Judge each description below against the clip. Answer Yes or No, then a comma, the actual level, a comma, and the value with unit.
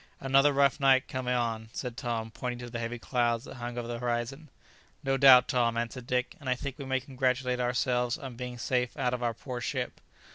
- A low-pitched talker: Yes, low, 125 Hz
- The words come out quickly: Yes, fast, 215 wpm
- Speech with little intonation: Yes, narrow, 1.7 semitones